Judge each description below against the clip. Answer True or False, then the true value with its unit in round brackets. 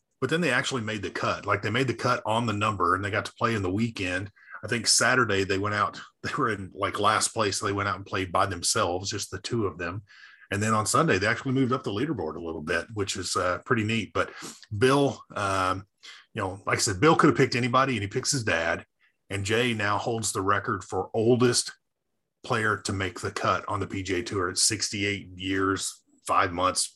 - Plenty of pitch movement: False (3.9 semitones)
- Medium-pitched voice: False (110 Hz)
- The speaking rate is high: True (235 wpm)